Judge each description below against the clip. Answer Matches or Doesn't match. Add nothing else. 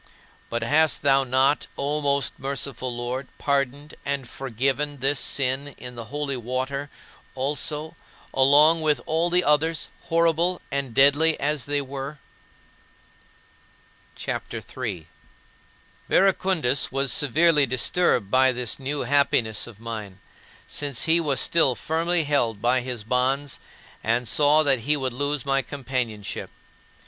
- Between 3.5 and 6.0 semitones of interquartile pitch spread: Doesn't match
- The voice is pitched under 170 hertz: Matches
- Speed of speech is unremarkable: Doesn't match